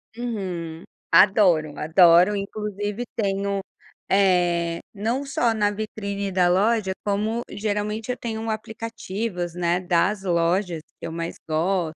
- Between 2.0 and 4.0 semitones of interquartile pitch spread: Yes, average, 3.5 semitones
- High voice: Yes, high, 200 Hz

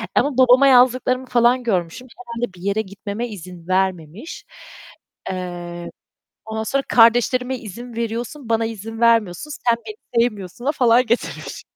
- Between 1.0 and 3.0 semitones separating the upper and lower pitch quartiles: No, average, 4.5 semitones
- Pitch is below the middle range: No, high, 230 Hz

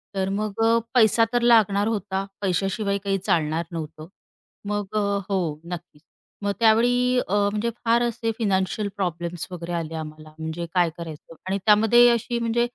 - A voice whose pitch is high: Yes, high, 200 Hz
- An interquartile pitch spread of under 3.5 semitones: No, average, 4.7 semitones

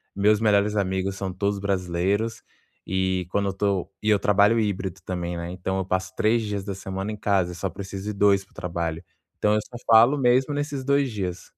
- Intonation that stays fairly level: Yes, narrow, 2.2 semitones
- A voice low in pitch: Yes, low, 100 Hz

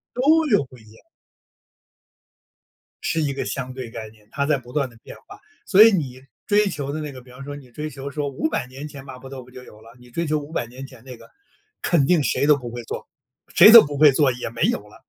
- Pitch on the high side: No, low, 135 Hz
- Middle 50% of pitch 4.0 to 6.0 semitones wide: No, average, 3.2 semitones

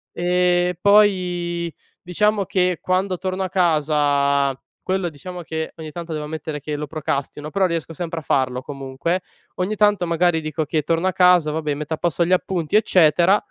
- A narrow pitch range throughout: No, average, 3.1 semitones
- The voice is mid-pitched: Yes, medium, 170 Hz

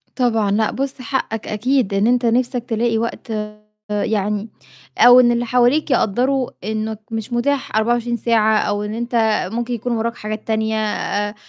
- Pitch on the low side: No, high, 230 Hz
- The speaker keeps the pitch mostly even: Yes, narrow, 2.1 semitones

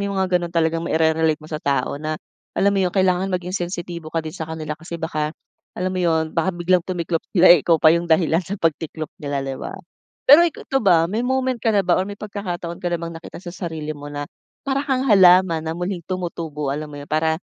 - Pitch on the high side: No, medium, 170 Hz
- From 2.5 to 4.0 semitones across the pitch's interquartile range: Yes, average, 2.8 semitones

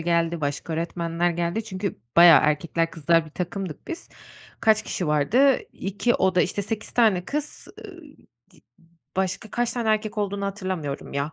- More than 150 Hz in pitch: Yes, medium, 185 Hz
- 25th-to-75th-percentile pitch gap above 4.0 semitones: Yes, average, 4.4 semitones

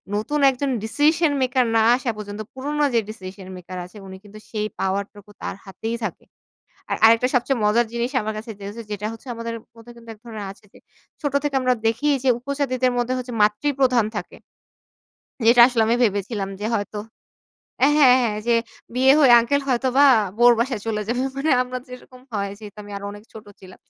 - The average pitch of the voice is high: Yes, high, 230 Hz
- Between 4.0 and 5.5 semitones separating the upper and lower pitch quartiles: No, average, 3.5 semitones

